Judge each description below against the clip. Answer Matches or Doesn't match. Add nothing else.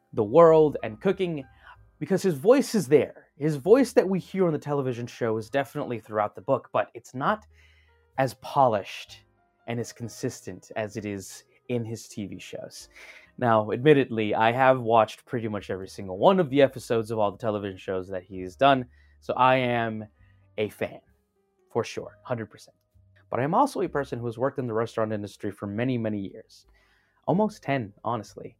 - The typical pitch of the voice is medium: Doesn't match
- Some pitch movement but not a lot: Doesn't match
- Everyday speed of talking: Matches